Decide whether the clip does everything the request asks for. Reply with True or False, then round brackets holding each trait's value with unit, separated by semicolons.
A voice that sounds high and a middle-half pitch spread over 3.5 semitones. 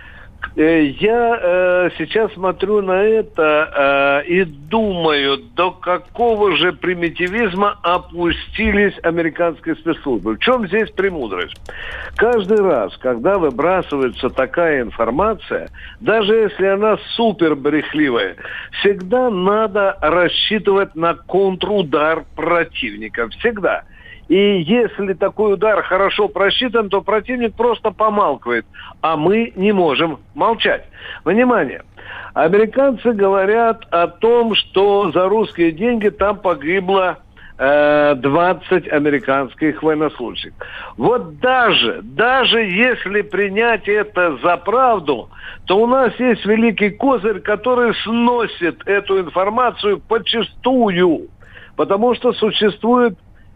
True (195 Hz; 4.6 semitones)